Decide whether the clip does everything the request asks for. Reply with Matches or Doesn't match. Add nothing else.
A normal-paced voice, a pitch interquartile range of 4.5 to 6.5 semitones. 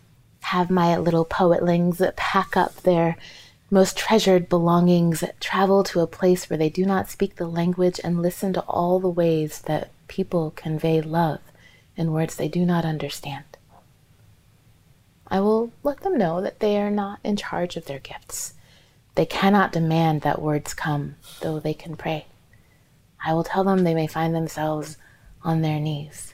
Doesn't match